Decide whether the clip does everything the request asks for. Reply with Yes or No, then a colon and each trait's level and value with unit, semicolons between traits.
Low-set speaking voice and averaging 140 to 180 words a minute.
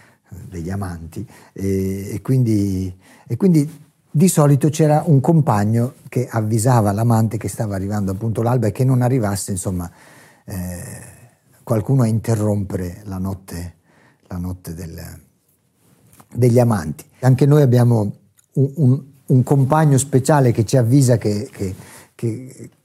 No: low, 115 Hz; average, 130 wpm